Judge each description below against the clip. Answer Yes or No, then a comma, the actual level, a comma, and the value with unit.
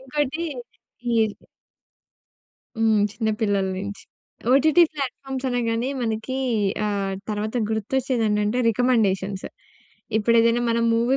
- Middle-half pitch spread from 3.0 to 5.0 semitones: Yes, average, 3.5 semitones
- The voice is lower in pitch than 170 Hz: No, high, 230 Hz